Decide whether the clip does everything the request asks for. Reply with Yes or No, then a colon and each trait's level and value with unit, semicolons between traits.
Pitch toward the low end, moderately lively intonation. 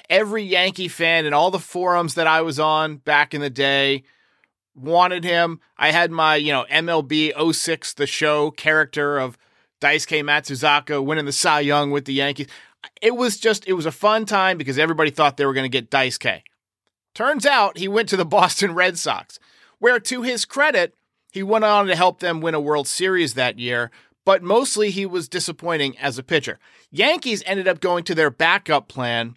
No: medium, 160 Hz; average, 4.4 semitones